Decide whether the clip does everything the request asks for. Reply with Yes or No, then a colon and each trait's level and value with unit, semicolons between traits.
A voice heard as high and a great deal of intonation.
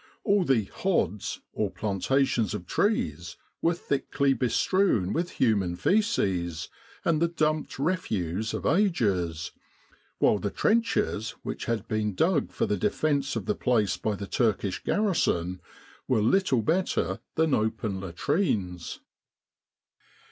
No: low, 115 Hz; wide, 9.0 semitones